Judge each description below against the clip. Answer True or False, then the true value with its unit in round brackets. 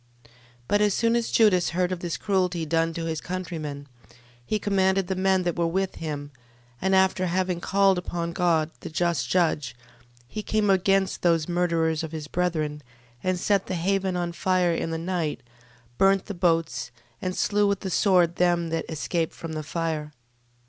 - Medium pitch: True (175 Hz)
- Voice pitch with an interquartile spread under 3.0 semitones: True (2.5 semitones)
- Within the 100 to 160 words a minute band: False (185 wpm)